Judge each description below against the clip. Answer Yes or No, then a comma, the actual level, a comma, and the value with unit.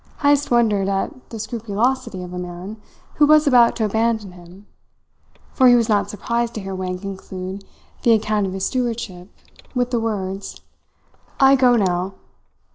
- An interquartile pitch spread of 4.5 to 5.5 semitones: No, average, 4.0 semitones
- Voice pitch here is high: Yes, high, 215 Hz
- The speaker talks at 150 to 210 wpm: Yes, average, 160 wpm